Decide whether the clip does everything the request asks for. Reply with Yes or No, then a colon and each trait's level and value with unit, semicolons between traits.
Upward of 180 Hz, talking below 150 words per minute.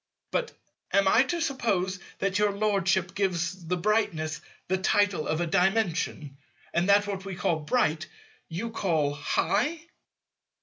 Yes: high, 190 Hz; average, 140 wpm